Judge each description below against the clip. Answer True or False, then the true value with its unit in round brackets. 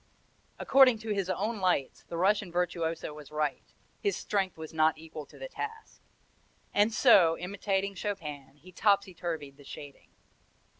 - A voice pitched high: False (180 Hz)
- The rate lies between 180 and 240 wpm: False (150 wpm)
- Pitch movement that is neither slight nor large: True (4.6 semitones)